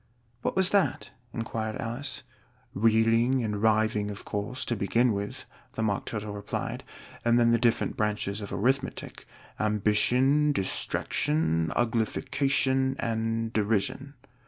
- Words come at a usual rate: No, slow, 120 wpm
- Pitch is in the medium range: No, low, 115 Hz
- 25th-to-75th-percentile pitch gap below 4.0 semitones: Yes, average, 3.5 semitones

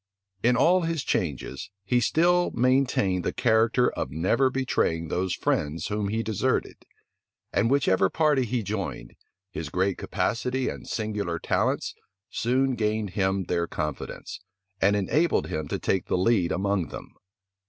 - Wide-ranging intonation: Yes, wide, 5.7 semitones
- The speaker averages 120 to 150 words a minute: Yes, average, 145 wpm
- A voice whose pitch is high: No, low, 105 Hz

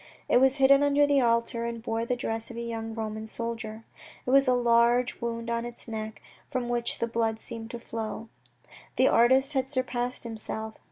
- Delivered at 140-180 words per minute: No, average, 190 wpm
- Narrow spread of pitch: Yes, narrow, 1.8 semitones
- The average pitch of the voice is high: Yes, high, 235 Hz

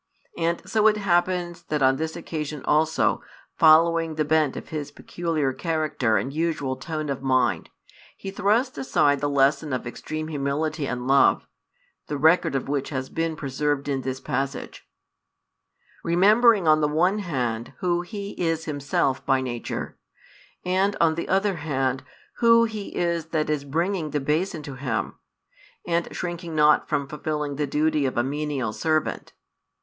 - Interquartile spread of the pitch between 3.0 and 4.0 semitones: Yes, average, 3.5 semitones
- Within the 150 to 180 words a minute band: Yes, average, 155 wpm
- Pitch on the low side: No, medium, 155 Hz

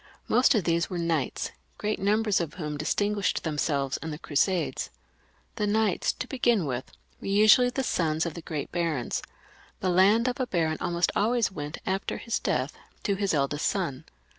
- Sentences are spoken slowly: No, average, 175 wpm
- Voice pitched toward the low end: No, medium, 180 Hz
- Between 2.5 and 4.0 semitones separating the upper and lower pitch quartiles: No, average, 5.1 semitones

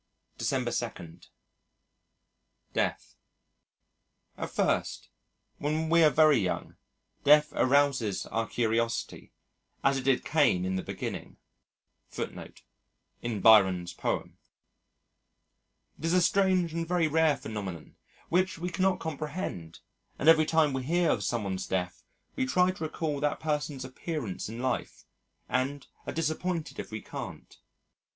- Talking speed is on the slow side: Yes, slow, 120 wpm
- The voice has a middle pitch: Yes, medium, 145 Hz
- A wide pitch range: Yes, wide, 6.1 semitones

